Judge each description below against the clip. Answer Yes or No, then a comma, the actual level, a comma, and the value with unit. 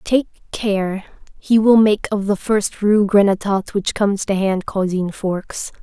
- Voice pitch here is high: Yes, high, 200 Hz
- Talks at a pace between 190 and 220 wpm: No, average, 165 wpm